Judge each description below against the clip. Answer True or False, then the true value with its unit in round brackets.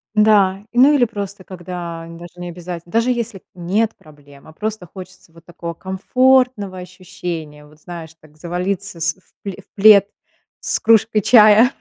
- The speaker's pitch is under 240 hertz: True (185 Hz)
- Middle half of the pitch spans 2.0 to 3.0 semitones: False (4.0 semitones)